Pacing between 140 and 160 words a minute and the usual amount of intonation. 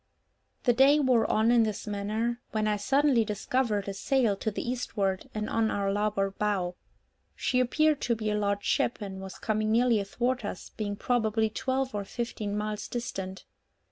No: average, 175 wpm; average, 3.1 semitones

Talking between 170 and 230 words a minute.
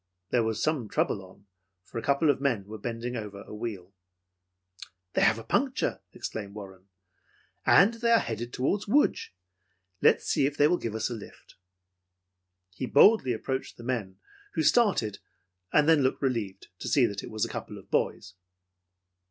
Yes: average, 175 wpm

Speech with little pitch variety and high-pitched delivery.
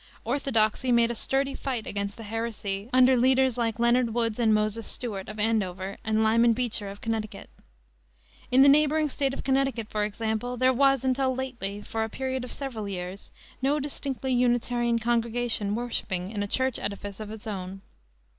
No: average, 3.4 semitones; high, 235 Hz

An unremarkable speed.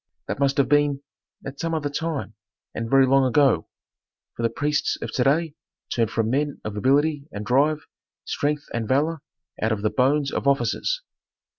Yes: average, 175 wpm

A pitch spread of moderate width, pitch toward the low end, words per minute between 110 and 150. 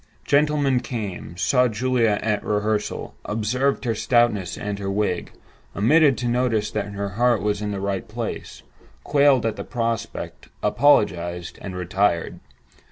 Yes: average, 3.7 semitones; low, 110 Hz; average, 140 wpm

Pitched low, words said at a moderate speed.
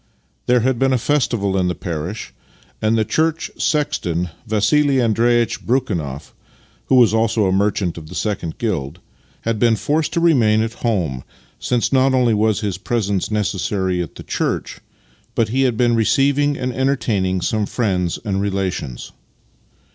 Yes: low, 110 Hz; average, 160 wpm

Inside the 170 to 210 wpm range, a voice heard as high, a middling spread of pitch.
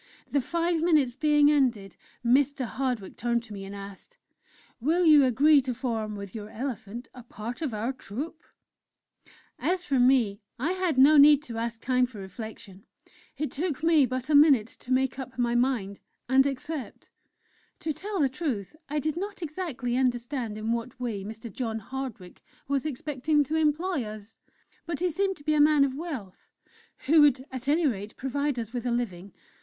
Yes: average, 180 wpm; very high, 260 Hz; average, 4.6 semitones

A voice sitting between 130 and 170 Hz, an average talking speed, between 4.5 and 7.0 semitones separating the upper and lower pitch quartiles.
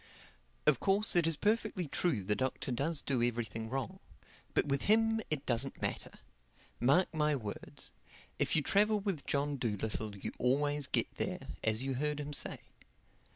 Yes: medium, 140 Hz; average, 160 wpm; wide, 5.6 semitones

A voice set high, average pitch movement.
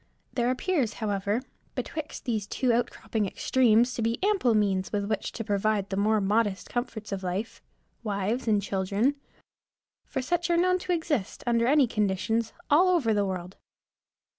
Yes: high, 225 Hz; average, 4.1 semitones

